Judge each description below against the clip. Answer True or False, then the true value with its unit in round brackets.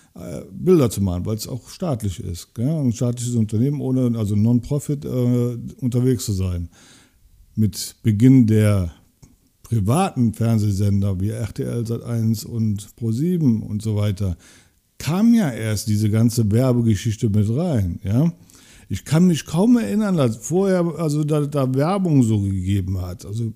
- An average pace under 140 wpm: True (130 wpm)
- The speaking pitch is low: True (115 Hz)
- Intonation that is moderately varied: True (4.1 semitones)